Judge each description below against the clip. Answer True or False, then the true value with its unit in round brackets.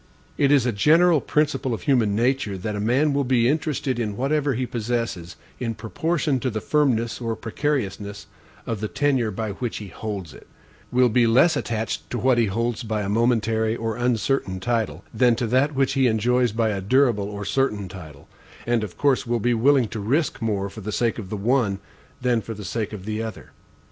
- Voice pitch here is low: True (115 Hz)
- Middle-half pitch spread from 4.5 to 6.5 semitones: False (3.5 semitones)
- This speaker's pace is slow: False (200 wpm)